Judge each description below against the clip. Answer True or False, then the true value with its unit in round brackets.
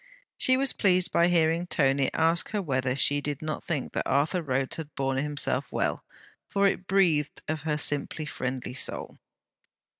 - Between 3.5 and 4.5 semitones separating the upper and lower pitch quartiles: True (3.9 semitones)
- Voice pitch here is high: False (150 Hz)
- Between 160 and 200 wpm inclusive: True (170 wpm)